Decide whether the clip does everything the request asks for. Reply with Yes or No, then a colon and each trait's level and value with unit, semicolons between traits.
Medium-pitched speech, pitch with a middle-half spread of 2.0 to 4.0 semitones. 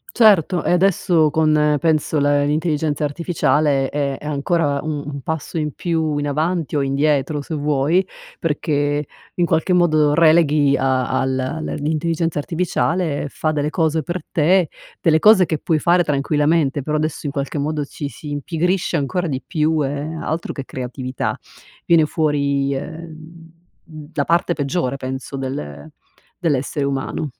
Yes: medium, 150 Hz; narrow, 2.5 semitones